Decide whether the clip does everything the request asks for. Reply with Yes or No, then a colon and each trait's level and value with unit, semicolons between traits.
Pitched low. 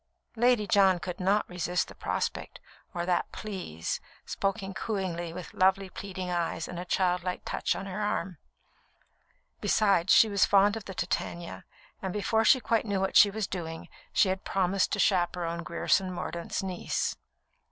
No: high, 190 Hz